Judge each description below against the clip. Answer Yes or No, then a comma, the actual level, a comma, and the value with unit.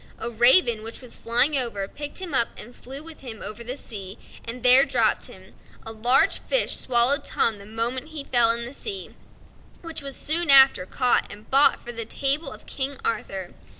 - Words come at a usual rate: Yes, average, 195 wpm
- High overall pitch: Yes, high, 245 Hz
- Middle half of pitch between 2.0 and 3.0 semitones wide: No, average, 3.5 semitones